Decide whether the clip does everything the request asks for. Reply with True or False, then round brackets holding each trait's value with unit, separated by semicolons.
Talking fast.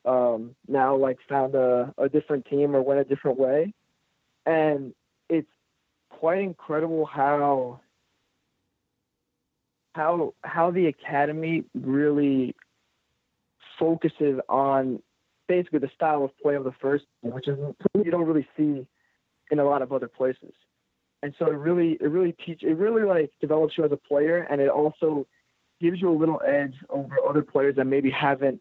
False (155 wpm)